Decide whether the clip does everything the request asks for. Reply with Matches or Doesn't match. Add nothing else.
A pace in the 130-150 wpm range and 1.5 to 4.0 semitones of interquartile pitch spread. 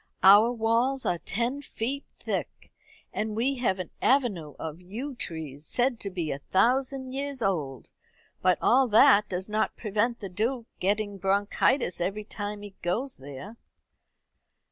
Doesn't match